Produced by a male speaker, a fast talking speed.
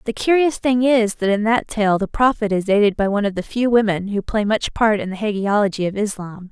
No: female; fast, 250 wpm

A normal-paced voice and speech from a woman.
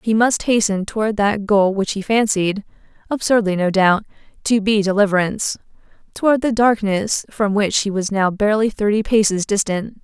Yes: average, 160 wpm; female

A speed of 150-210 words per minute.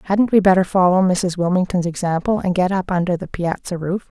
Yes: average, 200 wpm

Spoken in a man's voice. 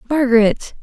No: female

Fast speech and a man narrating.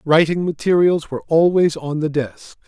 No: average, 155 wpm; male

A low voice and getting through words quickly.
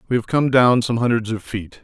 Yes: low, 115 Hz; fast, 260 wpm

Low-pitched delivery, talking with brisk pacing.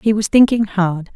No: high, 205 Hz; fast, 210 wpm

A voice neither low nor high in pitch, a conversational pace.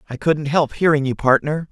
No: medium, 150 Hz; fast, 210 wpm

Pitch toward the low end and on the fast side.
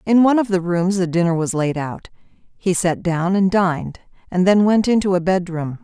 No: medium, 185 Hz; fast, 215 wpm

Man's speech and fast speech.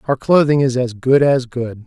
Yes: male; fast, 225 wpm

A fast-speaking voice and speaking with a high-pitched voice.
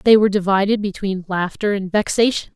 No: average, 165 wpm; high, 200 Hz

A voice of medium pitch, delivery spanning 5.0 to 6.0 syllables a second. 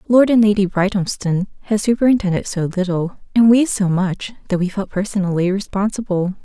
No: high, 200 Hz; 5.5 syllables/s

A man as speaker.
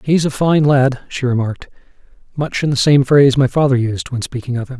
Yes: male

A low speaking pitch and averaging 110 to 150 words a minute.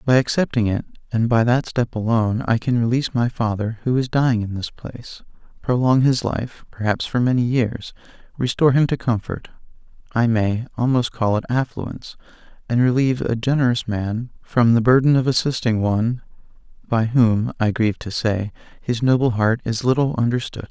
No: low, 120 Hz; average, 170 wpm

